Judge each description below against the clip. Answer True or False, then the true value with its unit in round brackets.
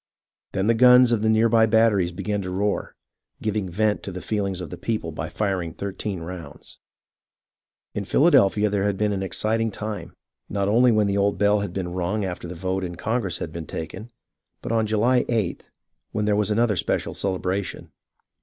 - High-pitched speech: False (100 Hz)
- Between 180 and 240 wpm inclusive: True (190 wpm)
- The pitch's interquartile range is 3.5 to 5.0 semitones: False (2.9 semitones)